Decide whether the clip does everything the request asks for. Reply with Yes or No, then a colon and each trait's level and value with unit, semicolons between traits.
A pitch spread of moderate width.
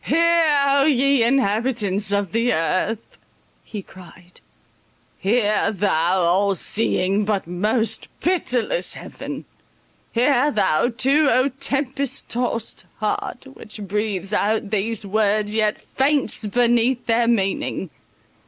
Yes: average, 4.4 semitones